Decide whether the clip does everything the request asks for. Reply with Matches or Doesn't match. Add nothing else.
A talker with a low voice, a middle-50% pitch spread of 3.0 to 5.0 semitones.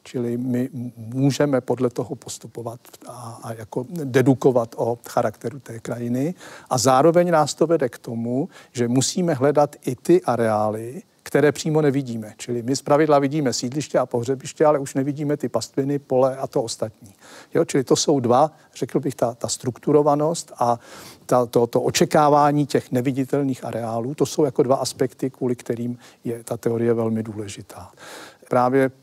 Matches